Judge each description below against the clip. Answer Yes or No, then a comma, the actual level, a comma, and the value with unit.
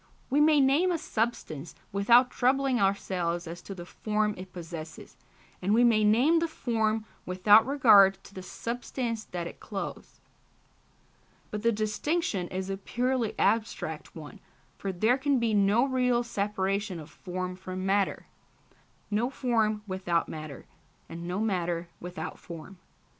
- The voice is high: Yes, high, 210 Hz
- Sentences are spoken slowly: No, average, 145 wpm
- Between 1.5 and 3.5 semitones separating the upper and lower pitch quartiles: No, average, 4.6 semitones